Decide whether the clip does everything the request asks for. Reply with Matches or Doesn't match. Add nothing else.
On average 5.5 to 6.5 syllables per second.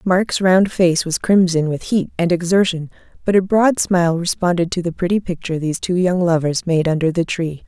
Doesn't match